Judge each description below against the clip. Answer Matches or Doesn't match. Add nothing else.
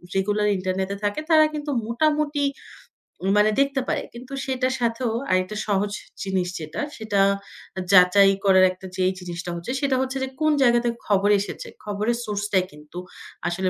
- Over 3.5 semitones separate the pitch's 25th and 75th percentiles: Matches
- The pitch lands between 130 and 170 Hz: Doesn't match